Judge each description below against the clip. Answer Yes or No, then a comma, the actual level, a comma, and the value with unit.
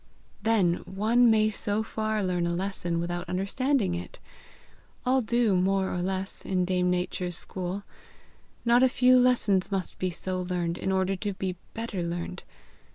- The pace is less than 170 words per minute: Yes, average, 160 wpm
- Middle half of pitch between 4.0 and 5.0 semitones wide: No, average, 3.3 semitones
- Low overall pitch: No, high, 190 Hz